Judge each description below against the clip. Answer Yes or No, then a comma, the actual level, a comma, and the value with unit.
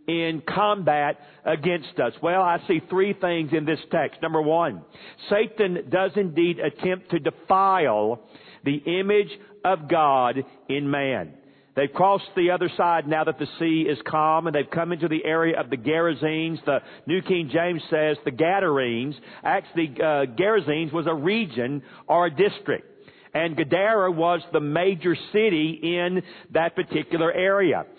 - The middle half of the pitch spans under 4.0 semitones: Yes, average, 3.0 semitones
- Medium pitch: Yes, medium, 165 Hz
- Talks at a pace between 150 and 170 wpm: Yes, average, 155 wpm